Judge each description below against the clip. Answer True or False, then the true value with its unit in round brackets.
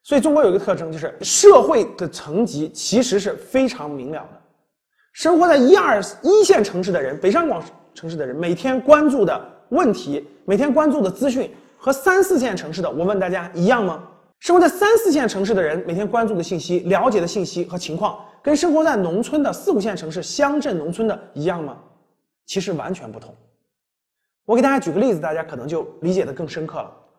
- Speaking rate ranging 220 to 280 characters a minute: False (310 characters per minute)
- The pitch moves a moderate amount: False (8.5 semitones)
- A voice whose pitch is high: True (205 Hz)